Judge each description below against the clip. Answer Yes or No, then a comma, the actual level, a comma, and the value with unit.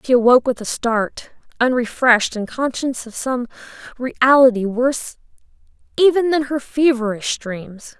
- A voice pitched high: Yes, very high, 250 Hz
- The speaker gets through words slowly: Yes, slow, 130 wpm